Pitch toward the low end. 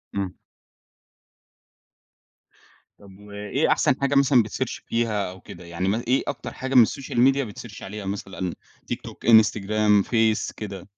Yes: low, 105 Hz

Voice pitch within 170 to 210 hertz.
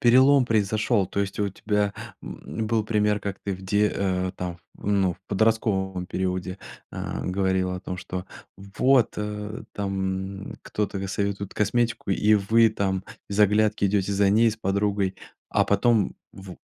No: low, 100 Hz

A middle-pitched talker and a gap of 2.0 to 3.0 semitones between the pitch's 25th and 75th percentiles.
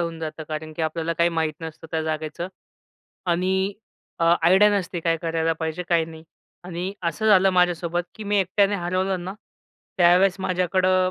Yes: medium, 175 Hz; narrow, 2.4 semitones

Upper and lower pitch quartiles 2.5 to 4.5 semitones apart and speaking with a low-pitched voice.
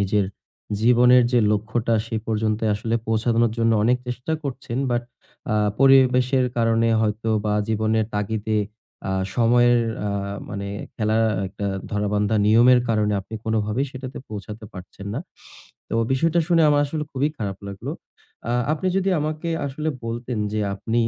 Yes: average, 2.9 semitones; low, 115 Hz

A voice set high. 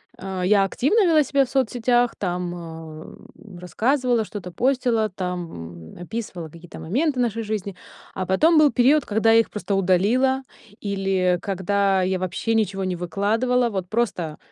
Yes: high, 200 Hz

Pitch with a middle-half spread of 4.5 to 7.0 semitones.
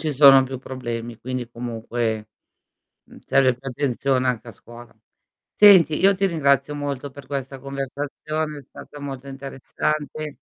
No: average, 2.7 semitones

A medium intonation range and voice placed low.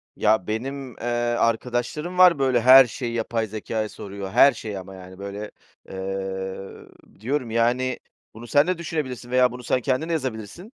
Yes: average, 4.1 semitones; low, 120 Hz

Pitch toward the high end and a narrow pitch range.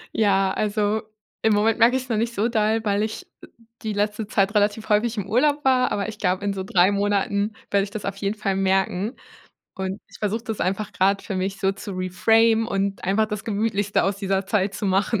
Yes: high, 205 Hz; narrow, 2.0 semitones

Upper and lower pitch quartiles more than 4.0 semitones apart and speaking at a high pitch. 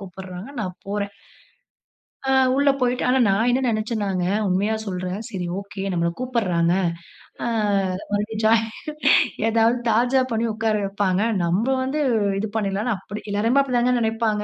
No: average, 3.4 semitones; high, 215 Hz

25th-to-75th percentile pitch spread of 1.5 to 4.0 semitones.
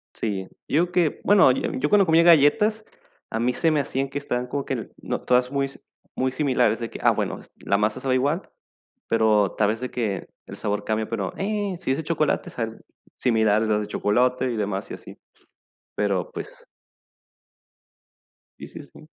No: average, 5.3 semitones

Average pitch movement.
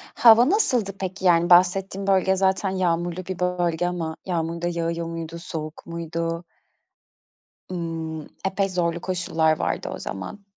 No: narrow, 2.2 semitones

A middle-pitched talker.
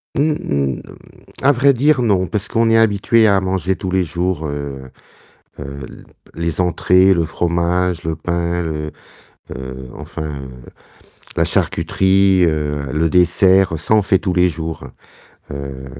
No: very low, 90 Hz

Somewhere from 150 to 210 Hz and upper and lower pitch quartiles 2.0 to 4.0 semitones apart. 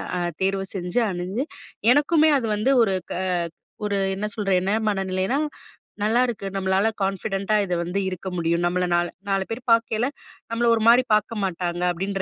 Yes: high, 195 Hz; average, 3.4 semitones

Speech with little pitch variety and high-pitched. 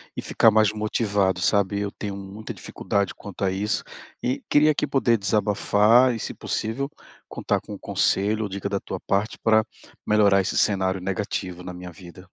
No: narrow, 2.2 semitones; low, 100 Hz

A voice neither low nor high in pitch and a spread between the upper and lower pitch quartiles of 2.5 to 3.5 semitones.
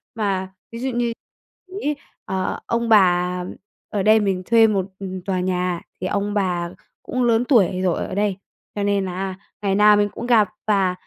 No: high, 200 Hz; average, 3.1 semitones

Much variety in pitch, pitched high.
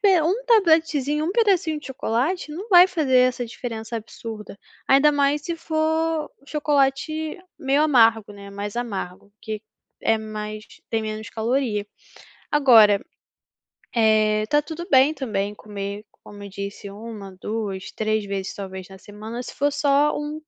Yes: wide, 6.2 semitones; high, 240 Hz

